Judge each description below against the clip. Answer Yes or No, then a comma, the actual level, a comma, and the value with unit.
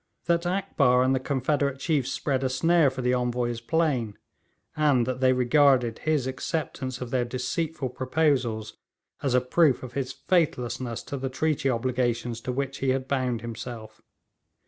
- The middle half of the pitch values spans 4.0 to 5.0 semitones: No, narrow, 2.5 semitones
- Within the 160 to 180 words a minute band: Yes, average, 165 wpm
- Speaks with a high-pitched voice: No, low, 130 Hz